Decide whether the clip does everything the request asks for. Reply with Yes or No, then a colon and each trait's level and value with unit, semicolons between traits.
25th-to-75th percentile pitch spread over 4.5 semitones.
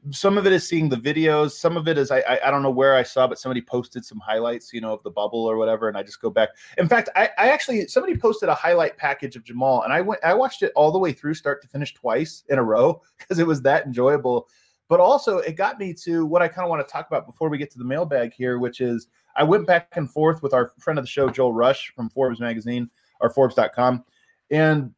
Yes: average, 4.9 semitones